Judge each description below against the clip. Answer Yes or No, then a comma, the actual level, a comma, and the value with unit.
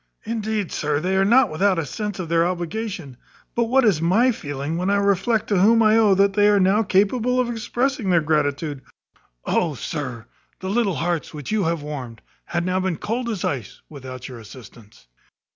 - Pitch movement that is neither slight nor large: No, wide, 6.1 semitones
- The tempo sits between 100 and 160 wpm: No, average, 195 wpm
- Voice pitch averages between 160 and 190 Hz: Yes, medium, 185 Hz